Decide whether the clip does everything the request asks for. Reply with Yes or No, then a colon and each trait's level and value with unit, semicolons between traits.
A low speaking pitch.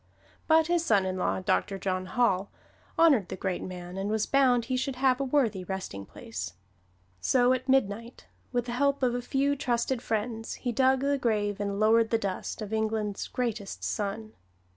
No: high, 225 Hz